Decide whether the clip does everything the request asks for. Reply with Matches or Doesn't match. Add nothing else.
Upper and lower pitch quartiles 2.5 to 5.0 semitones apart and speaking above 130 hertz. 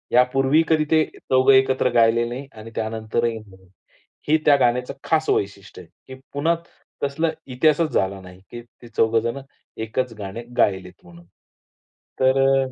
Doesn't match